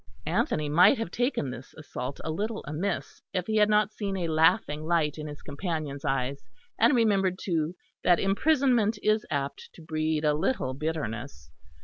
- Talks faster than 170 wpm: No, average, 165 wpm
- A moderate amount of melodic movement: No, wide, 5.8 semitones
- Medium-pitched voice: Yes, medium, 160 Hz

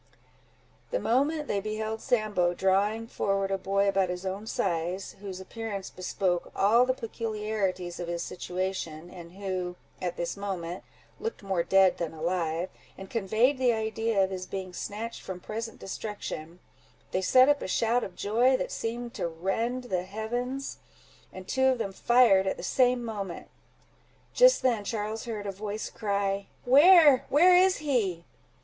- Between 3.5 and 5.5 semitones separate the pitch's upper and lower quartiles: Yes, average, 3.9 semitones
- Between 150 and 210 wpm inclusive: Yes, average, 160 wpm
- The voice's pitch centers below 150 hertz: No, high, 200 Hz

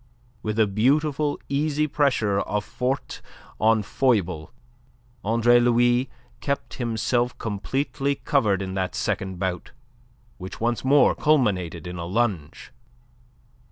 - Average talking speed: No, slow, 115 wpm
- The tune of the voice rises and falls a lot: Yes, wide, 5.7 semitones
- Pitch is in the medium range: No, low, 115 Hz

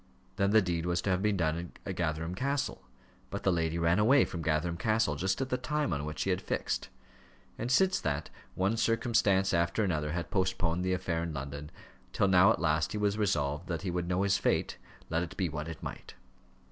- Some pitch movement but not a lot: Yes, average, 3.7 semitones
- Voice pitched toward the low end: Yes, very low, 90 Hz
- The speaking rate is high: Yes, fast, 215 wpm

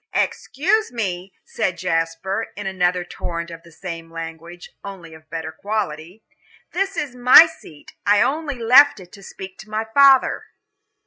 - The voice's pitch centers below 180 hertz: No, high, 190 Hz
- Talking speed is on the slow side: No, average, 155 wpm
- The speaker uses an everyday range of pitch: No, wide, 6.7 semitones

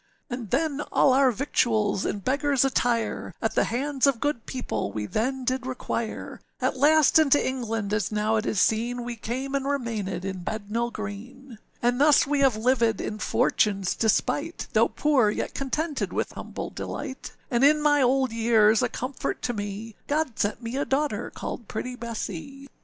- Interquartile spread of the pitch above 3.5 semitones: Yes, average, 4.0 semitones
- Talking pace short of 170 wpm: No, average, 175 wpm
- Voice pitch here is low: No, high, 245 Hz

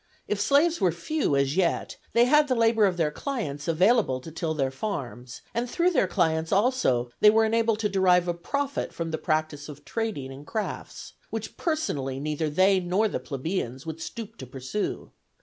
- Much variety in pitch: Yes, wide, 7.3 semitones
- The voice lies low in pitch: No, medium, 180 Hz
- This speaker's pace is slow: No, average, 185 wpm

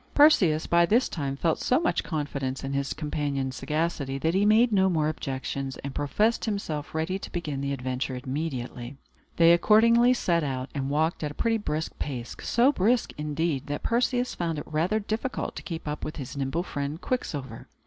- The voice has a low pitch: No, medium, 155 Hz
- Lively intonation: Yes, wide, 5.8 semitones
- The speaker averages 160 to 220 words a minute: Yes, average, 185 wpm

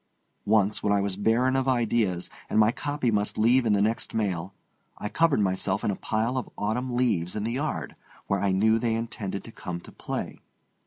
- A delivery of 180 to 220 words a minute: Yes, fast, 205 wpm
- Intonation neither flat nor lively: Yes, average, 3.2 semitones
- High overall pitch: No, low, 110 Hz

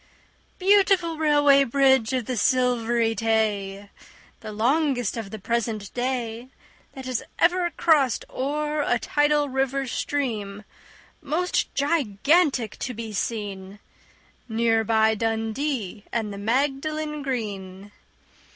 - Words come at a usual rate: No, slow, 110 wpm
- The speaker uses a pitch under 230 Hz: No, high, 245 Hz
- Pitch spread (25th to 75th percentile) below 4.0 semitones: No, average, 4.7 semitones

